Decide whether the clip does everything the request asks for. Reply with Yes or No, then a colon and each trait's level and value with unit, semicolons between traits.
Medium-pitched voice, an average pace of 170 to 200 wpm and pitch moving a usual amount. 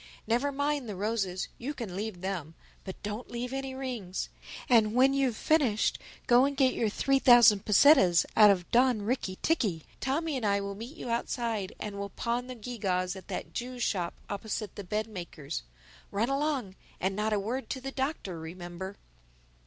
No: high, 220 Hz; average, 175 wpm; average, 4.8 semitones